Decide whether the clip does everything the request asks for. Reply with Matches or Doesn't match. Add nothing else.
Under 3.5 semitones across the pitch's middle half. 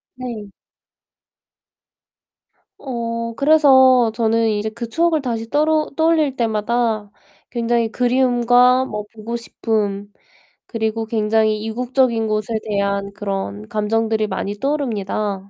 Matches